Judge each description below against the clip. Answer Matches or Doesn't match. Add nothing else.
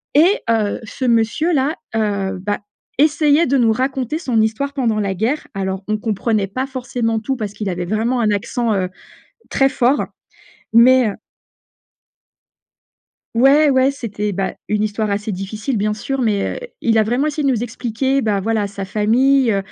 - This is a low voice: Doesn't match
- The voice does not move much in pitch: Doesn't match